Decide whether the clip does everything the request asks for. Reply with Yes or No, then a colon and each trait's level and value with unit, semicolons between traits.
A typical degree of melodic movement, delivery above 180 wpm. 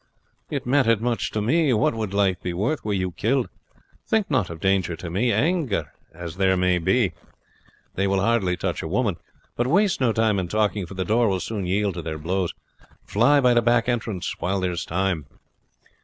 Yes: average, 4.6 semitones; fast, 205 wpm